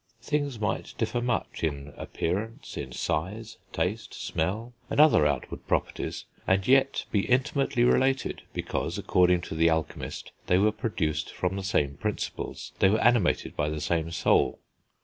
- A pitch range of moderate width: No, wide, 6.8 semitones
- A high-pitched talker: No, very low, 95 Hz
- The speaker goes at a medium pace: Yes, average, 150 wpm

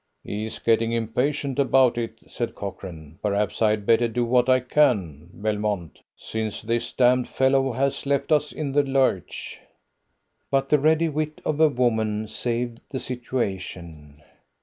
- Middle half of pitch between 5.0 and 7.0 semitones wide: No, average, 4.3 semitones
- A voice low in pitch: Yes, low, 120 Hz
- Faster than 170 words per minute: No, average, 150 wpm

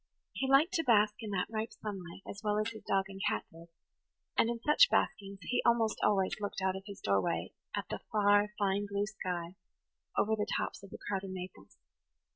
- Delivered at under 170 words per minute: No, average, 200 wpm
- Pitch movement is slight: Yes, narrow, 2.3 semitones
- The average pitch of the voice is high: Yes, high, 205 Hz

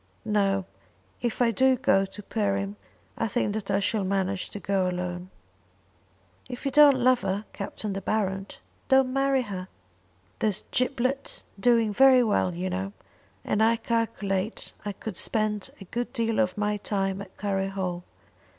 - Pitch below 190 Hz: No, high, 205 Hz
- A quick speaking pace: No, average, 160 wpm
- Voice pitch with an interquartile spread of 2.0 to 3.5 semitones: Yes, average, 3.2 semitones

